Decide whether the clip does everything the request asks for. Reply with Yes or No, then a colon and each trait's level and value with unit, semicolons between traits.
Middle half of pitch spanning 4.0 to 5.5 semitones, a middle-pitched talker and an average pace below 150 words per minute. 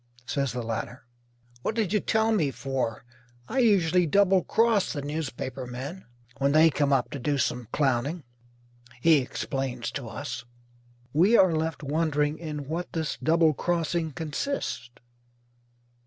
Yes: average, 4.3 semitones; medium, 150 Hz; average, 140 wpm